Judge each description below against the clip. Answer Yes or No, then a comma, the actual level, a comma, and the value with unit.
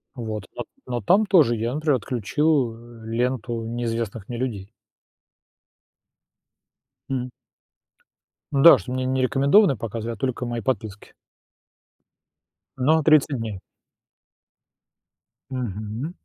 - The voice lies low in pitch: Yes, low, 120 Hz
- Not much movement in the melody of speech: No, average, 3.1 semitones